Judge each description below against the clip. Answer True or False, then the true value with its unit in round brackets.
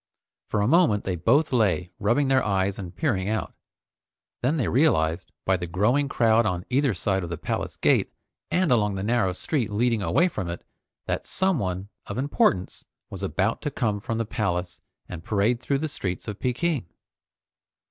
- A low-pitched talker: True (110 Hz)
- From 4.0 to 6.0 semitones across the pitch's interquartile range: True (5.6 semitones)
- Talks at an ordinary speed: True (180 wpm)